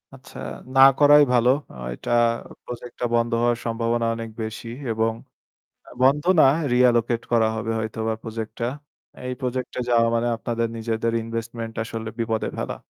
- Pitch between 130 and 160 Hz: No, low, 115 Hz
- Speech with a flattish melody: Yes, narrow, 1.4 semitones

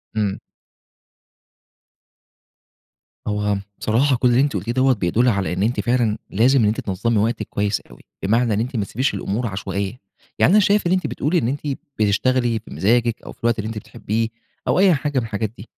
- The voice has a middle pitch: No, low, 115 Hz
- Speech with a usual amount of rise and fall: Yes, average, 3.7 semitones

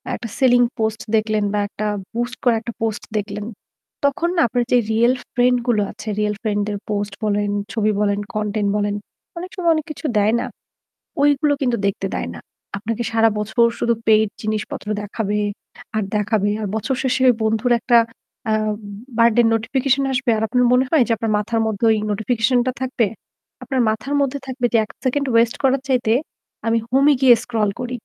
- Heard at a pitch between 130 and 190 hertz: No, high, 230 Hz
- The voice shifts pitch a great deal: No, average, 3.0 semitones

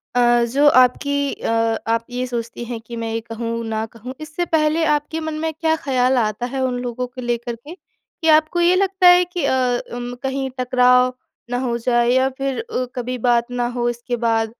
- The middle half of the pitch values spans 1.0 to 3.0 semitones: No, average, 3.4 semitones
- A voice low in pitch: No, very high, 250 Hz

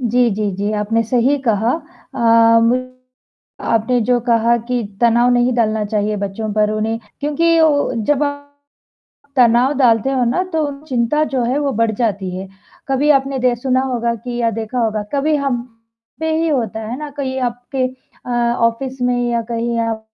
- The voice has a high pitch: Yes, high, 240 Hz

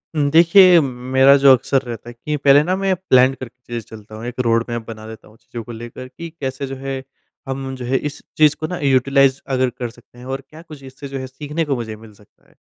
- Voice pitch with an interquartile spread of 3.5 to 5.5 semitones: No, average, 3.0 semitones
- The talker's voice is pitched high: No, low, 130 Hz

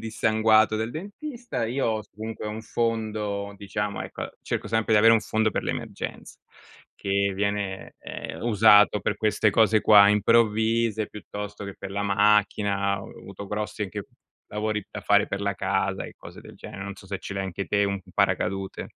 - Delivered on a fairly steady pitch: Yes, narrow, 1.6 semitones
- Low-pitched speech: Yes, low, 105 Hz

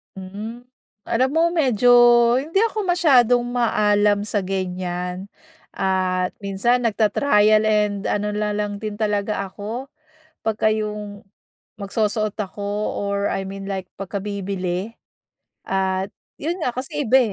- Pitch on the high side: Yes, high, 210 Hz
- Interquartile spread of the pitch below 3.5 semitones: Yes, average, 2.9 semitones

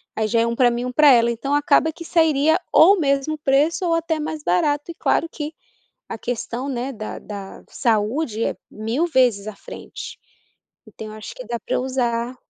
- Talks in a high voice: Yes, very high, 260 Hz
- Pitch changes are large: No, average, 4.7 semitones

